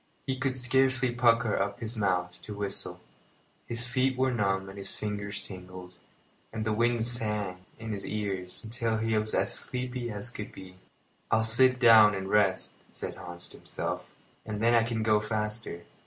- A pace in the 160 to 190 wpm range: Yes, average, 180 wpm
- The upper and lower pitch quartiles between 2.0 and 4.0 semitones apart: Yes, average, 3.1 semitones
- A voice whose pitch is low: Yes, low, 110 Hz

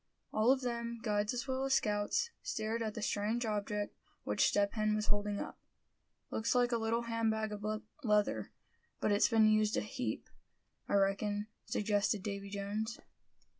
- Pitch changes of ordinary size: No, narrow, 1.9 semitones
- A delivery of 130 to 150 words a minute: No, average, 170 wpm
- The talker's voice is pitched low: No, high, 215 Hz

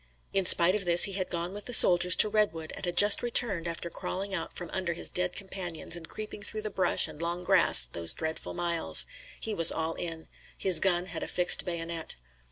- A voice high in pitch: No, medium, 175 Hz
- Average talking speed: No, fast, 215 wpm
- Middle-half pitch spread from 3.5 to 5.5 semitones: No, narrow, 2.6 semitones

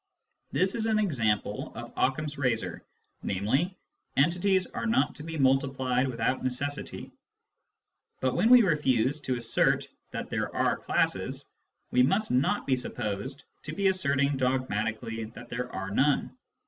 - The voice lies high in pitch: No, low, 135 Hz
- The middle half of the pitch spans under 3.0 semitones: No, average, 4.4 semitones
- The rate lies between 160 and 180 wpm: No, average, 145 wpm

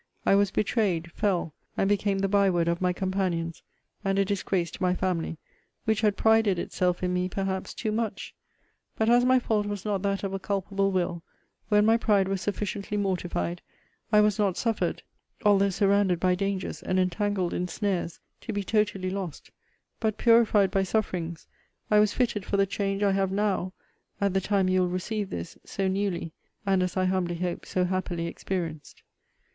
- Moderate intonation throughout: No, narrow, 2.1 semitones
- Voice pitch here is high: Yes, high, 195 Hz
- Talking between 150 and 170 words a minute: No, average, 185 wpm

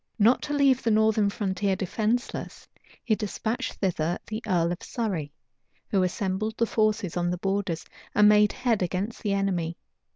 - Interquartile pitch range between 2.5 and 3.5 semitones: Yes, average, 3.1 semitones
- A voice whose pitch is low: No, high, 205 Hz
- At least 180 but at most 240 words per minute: No, average, 160 wpm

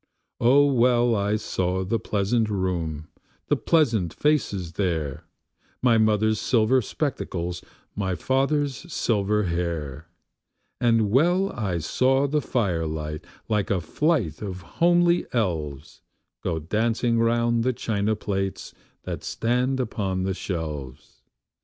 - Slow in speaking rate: Yes, slow, 115 wpm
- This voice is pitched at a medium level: No, low, 105 Hz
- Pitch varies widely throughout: Yes, wide, 5.7 semitones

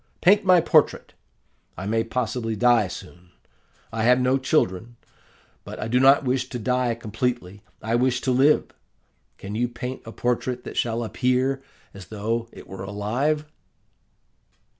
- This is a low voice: Yes, low, 120 Hz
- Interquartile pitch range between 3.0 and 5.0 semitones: No, narrow, 2.6 semitones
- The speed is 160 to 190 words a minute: No, average, 150 wpm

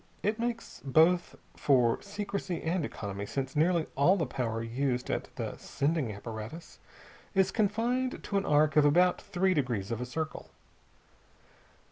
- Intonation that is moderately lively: No, wide, 7.4 semitones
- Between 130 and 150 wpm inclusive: Yes, average, 145 wpm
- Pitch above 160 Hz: No, medium, 155 Hz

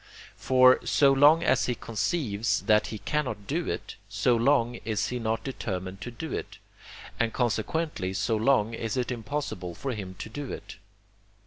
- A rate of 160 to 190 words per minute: Yes, average, 170 wpm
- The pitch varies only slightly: No, average, 4.3 semitones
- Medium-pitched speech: No, low, 120 Hz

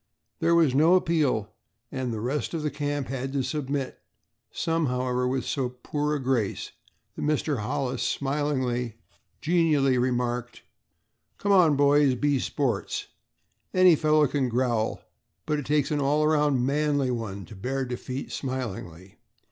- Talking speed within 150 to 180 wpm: No, average, 140 wpm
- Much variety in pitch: No, average, 3.1 semitones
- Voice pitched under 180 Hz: Yes, low, 135 Hz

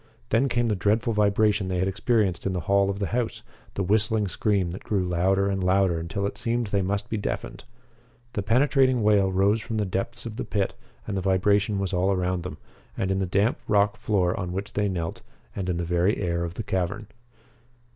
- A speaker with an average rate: No, fast, 210 wpm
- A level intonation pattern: Yes, narrow, 2.3 semitones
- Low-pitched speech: Yes, low, 100 Hz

